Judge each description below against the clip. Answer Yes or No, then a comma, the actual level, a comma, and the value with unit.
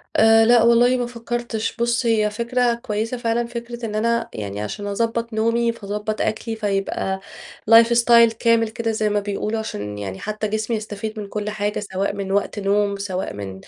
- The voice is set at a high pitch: Yes, high, 220 Hz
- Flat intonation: Yes, narrow, 2.3 semitones